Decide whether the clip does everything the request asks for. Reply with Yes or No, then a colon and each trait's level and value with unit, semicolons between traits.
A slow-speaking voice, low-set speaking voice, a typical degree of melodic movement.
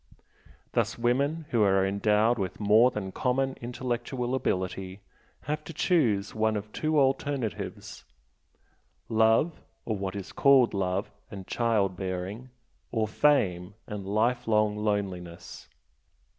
Yes: slow, 115 wpm; low, 110 Hz; average, 4.2 semitones